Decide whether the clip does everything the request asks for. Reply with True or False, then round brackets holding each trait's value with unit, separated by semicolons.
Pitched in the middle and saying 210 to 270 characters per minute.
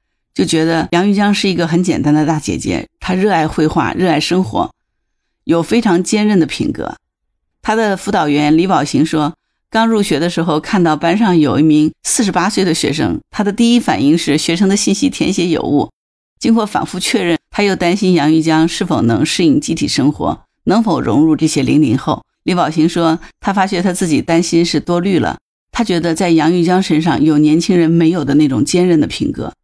False (170 Hz; 300 characters per minute)